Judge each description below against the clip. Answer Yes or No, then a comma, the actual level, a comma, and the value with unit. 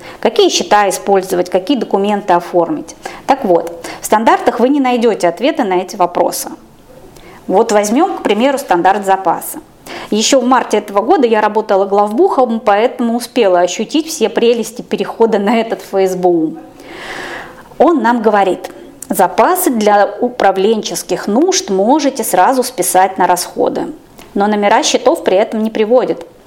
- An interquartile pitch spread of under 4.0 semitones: No, average, 4.7 semitones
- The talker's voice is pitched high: Yes, high, 215 Hz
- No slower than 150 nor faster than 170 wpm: No, average, 135 wpm